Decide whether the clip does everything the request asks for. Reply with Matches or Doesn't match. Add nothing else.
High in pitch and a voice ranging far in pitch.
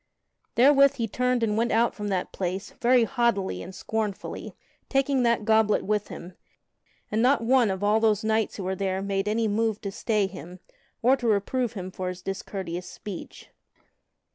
Doesn't match